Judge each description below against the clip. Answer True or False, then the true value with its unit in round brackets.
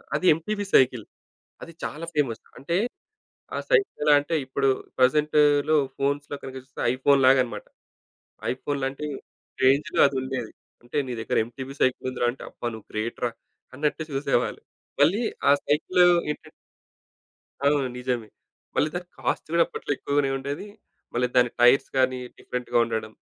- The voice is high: False (135 Hz)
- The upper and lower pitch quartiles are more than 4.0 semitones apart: False (3.0 semitones)